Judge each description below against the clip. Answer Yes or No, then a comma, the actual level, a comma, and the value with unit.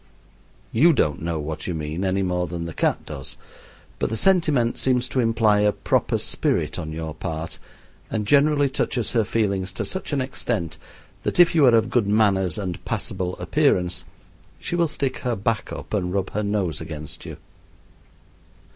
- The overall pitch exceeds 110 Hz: No, low, 100 Hz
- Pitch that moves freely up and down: Yes, wide, 6.1 semitones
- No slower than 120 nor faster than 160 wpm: No, average, 175 wpm